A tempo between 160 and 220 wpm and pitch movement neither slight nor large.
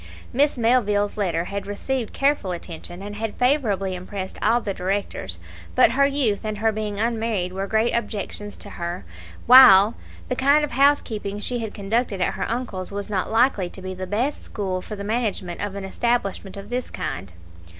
Yes: average, 180 wpm; average, 3.7 semitones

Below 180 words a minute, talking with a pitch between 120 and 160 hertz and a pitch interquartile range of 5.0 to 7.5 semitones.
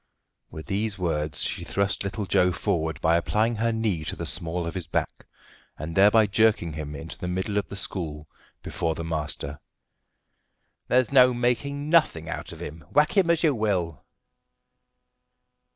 No: average, 165 wpm; very low, 95 Hz; wide, 5.6 semitones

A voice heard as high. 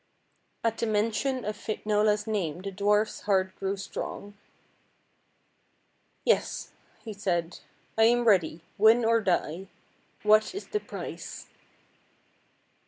Yes: high, 210 Hz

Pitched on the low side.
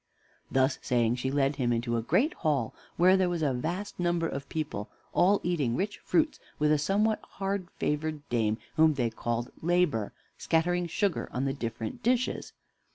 No: medium, 150 Hz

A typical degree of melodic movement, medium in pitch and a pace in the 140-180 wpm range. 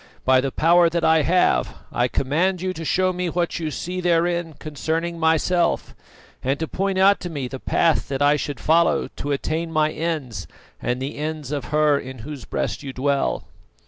No: average, 3.4 semitones; medium, 160 Hz; average, 190 wpm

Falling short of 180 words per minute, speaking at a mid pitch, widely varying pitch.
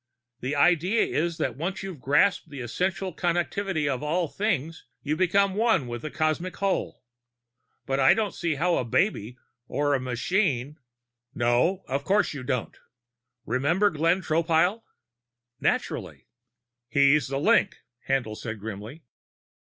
Yes: average, 140 wpm; medium, 155 Hz; wide, 5.7 semitones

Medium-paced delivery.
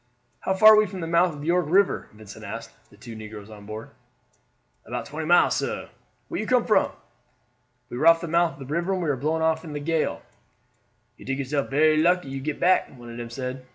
No: fast, 230 wpm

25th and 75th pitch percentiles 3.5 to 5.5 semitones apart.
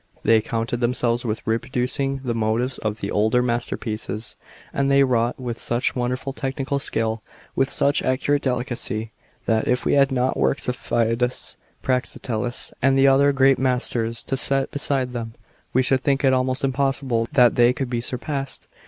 No: narrow, 2.4 semitones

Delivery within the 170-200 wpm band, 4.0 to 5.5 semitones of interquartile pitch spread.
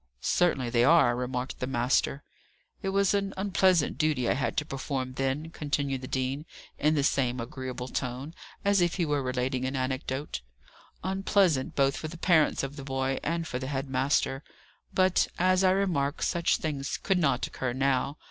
Yes: average, 175 wpm; average, 4.4 semitones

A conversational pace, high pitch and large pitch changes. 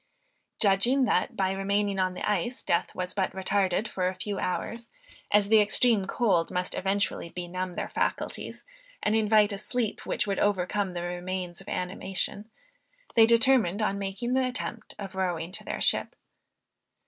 No: average, 160 wpm; high, 195 Hz; average, 2.7 semitones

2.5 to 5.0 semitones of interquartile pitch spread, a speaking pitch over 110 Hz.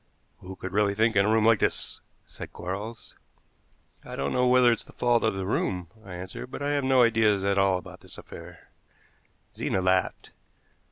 No: average, 3.6 semitones; low, 105 Hz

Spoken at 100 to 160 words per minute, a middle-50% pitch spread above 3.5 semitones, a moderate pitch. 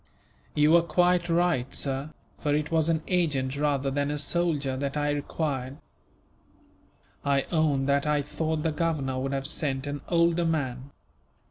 No: average, 155 wpm; average, 3.0 semitones; medium, 145 Hz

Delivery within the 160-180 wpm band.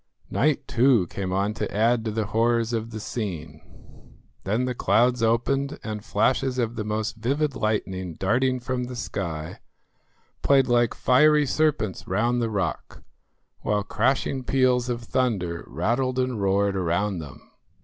No: average, 150 wpm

